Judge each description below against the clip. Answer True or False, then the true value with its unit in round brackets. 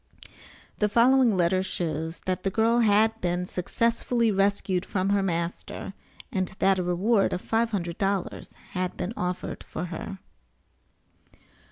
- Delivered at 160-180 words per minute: False (140 wpm)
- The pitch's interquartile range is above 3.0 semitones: True (3.7 semitones)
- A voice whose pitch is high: True (195 Hz)